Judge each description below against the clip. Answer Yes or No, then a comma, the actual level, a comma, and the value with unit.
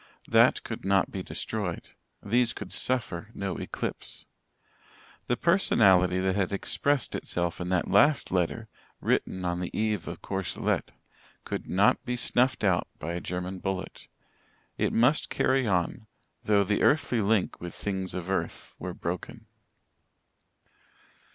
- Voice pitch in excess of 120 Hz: No, very low, 95 Hz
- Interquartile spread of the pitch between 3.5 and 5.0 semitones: Yes, average, 4.0 semitones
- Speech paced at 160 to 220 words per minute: No, average, 140 wpm